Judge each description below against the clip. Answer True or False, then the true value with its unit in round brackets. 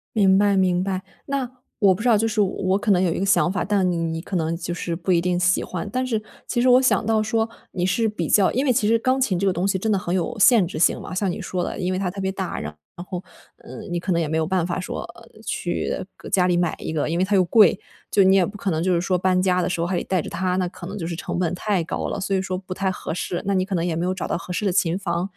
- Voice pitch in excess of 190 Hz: False (185 Hz)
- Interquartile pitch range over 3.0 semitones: False (2.5 semitones)